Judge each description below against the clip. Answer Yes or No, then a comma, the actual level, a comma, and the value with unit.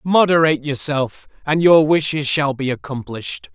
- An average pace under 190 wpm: Yes, slow, 135 wpm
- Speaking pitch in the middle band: Yes, medium, 145 Hz